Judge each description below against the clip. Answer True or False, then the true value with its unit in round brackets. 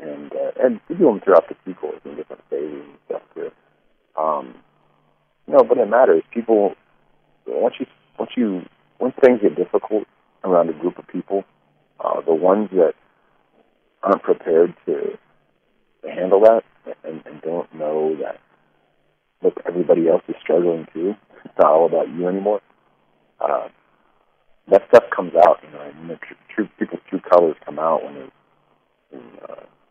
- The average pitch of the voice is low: True (110 Hz)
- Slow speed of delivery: False (165 wpm)